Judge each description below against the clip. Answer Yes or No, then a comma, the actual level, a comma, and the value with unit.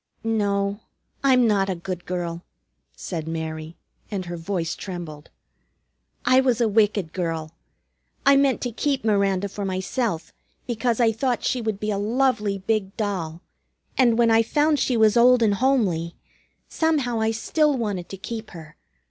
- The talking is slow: No, average, 155 wpm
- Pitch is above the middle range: Yes, high, 210 Hz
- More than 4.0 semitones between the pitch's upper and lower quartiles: Yes, average, 4.7 semitones